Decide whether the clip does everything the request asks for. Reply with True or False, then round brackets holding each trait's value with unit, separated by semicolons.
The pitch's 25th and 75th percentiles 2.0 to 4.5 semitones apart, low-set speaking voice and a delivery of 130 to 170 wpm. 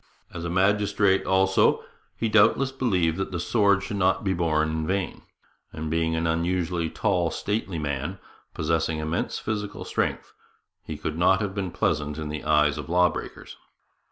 True (3.8 semitones; 90 Hz; 165 wpm)